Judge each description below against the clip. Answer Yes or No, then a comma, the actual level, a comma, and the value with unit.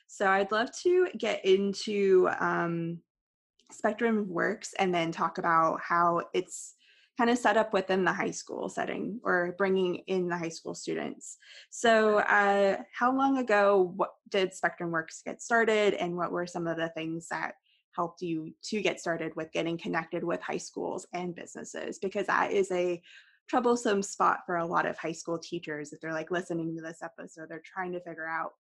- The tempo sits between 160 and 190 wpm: Yes, average, 185 wpm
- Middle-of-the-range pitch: Yes, medium, 180 Hz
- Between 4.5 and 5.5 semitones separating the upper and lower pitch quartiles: No, average, 3.7 semitones